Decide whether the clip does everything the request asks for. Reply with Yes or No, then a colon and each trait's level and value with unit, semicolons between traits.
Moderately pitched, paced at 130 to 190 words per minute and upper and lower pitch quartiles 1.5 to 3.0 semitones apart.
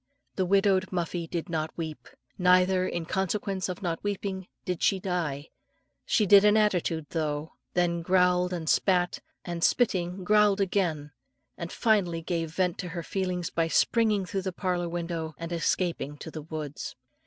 Yes: medium, 180 Hz; average, 160 wpm; narrow, 2.4 semitones